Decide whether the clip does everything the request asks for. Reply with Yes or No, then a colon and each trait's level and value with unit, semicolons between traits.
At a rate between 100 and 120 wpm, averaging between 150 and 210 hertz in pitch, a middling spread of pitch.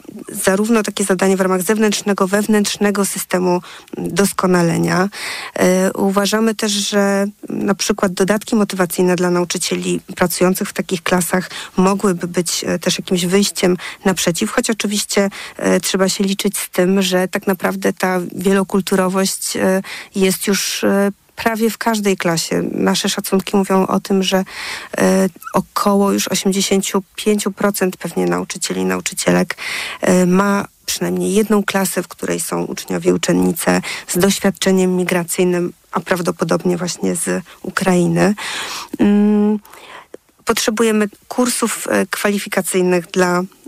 No: average, 115 wpm; high, 190 Hz; narrow, 2.0 semitones